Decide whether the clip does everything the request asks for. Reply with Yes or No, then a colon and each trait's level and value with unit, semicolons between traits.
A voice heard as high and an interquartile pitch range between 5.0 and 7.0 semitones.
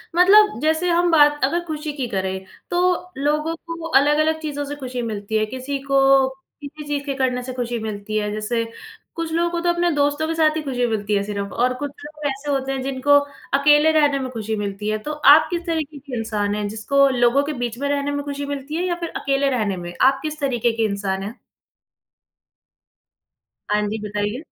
Yes: very high, 275 Hz; wide, 5.4 semitones